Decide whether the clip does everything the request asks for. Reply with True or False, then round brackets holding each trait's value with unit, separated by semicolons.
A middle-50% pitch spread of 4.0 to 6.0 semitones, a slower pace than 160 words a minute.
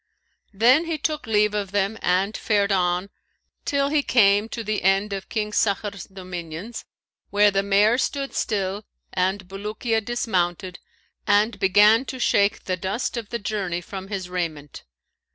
False (2.7 semitones; 150 wpm)